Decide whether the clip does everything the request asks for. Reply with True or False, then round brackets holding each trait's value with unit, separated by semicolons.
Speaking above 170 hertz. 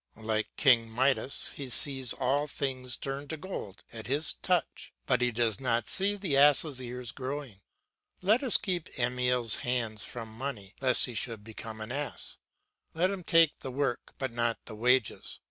False (125 Hz)